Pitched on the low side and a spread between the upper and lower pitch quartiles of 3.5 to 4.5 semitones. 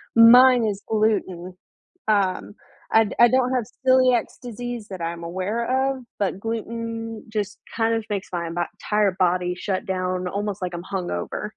No: high, 210 Hz; average, 3.9 semitones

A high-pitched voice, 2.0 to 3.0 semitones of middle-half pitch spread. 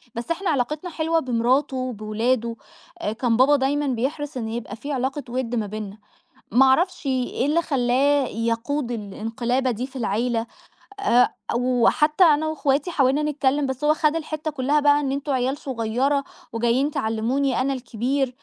No: very high, 265 Hz; average, 3.5 semitones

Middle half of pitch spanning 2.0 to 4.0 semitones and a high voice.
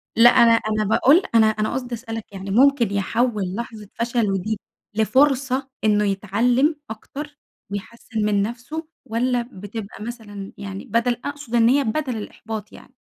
Yes: average, 3.1 semitones; high, 225 Hz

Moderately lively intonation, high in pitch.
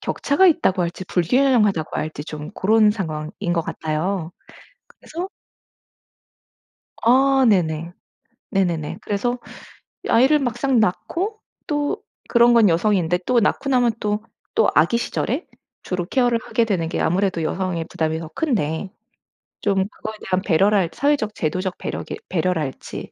No: wide, 6.3 semitones; high, 200 Hz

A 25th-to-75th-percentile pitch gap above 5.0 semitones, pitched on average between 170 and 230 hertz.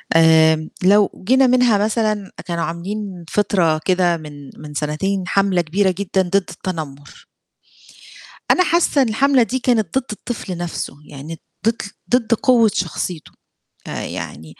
Yes: wide, 5.5 semitones; high, 190 Hz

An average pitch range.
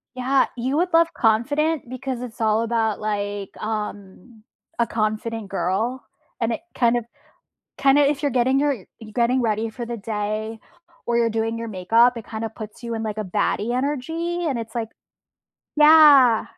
Yes: average, 3.3 semitones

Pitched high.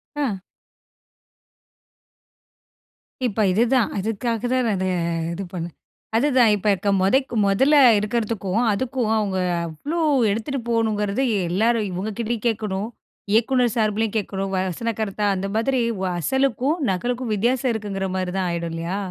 Yes: high, 220 Hz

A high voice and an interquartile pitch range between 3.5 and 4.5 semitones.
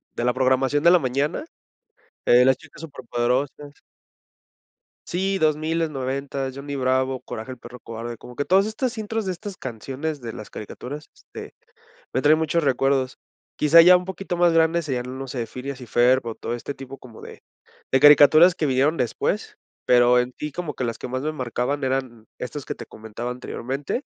No: low, 135 Hz; average, 3.8 semitones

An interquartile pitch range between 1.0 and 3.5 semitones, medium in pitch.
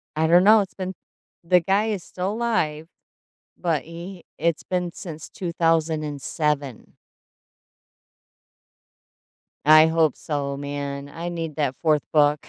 Yes: average, 3.1 semitones; medium, 160 Hz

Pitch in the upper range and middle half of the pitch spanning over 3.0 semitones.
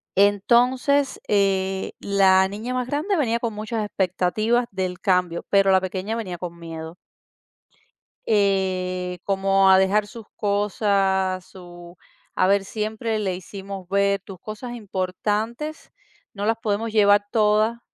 No: high, 200 Hz; average, 2.7 semitones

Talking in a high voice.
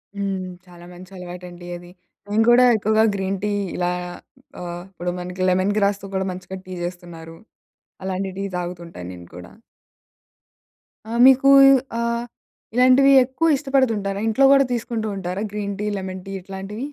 Yes: high, 195 Hz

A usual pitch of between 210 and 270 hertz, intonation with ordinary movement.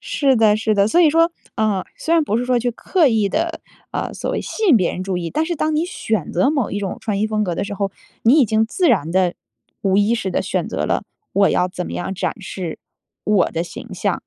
No: high, 215 Hz; wide, 6.5 semitones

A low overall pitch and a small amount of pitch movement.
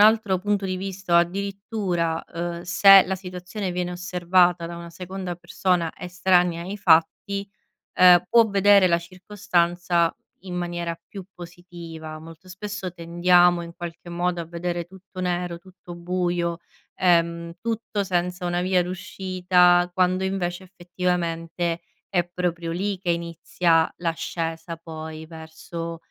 No: medium, 175 Hz; narrow, 1.6 semitones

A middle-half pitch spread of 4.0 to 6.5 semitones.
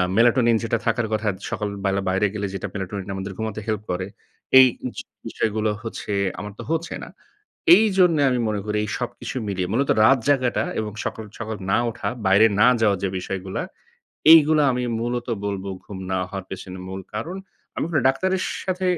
Yes: average, 4.4 semitones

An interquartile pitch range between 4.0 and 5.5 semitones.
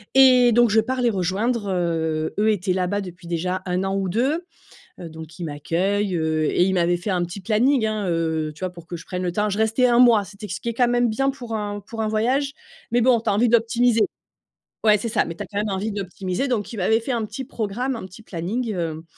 Yes: average, 4.7 semitones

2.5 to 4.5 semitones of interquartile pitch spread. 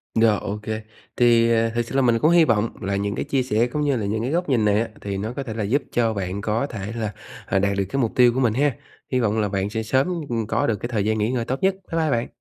Yes: average, 3.3 semitones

